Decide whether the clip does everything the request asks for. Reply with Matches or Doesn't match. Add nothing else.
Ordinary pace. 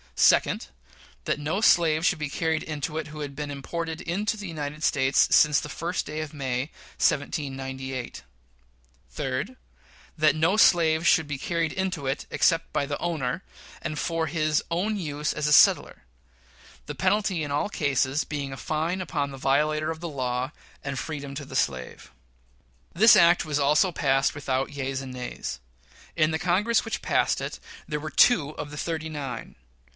Matches